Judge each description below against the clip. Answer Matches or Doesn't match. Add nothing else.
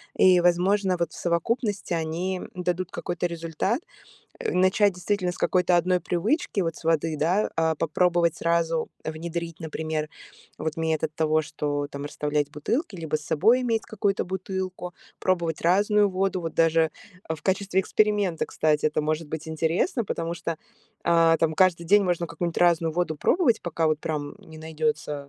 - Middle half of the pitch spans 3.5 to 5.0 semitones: Doesn't match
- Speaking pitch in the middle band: Matches